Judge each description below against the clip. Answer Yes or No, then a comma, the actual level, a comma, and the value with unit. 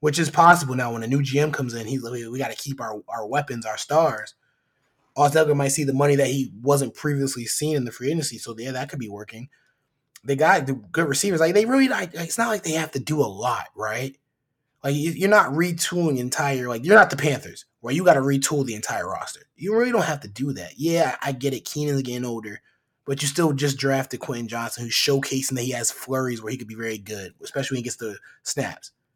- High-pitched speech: No, low, 135 Hz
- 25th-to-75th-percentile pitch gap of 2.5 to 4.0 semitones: Yes, average, 3.6 semitones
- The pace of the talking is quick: Yes, fast, 245 wpm